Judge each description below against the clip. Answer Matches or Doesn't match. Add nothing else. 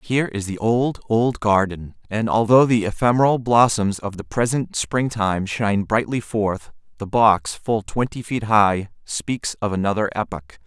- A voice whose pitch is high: Doesn't match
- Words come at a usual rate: Matches